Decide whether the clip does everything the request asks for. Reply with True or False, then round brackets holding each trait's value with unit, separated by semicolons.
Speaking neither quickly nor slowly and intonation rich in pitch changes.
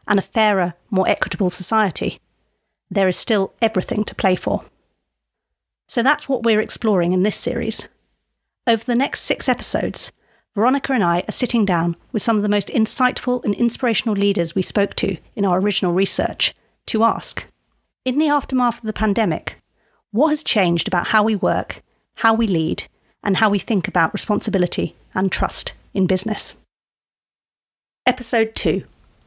False (160 wpm; 3.5 semitones)